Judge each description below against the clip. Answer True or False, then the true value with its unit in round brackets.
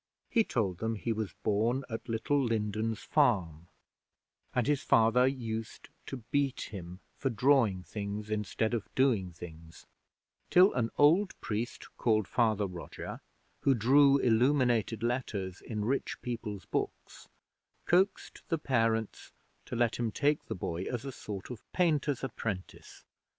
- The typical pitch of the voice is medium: False (115 Hz)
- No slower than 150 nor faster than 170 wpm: False (140 wpm)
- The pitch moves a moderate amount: True (4.0 semitones)